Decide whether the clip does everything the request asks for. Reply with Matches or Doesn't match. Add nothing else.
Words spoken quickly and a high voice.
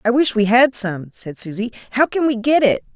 Matches